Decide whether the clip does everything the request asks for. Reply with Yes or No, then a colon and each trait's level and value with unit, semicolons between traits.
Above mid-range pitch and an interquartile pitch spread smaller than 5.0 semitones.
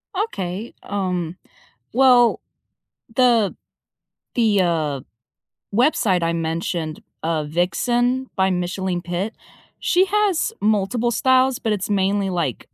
No: high, 195 Hz; wide, 5.6 semitones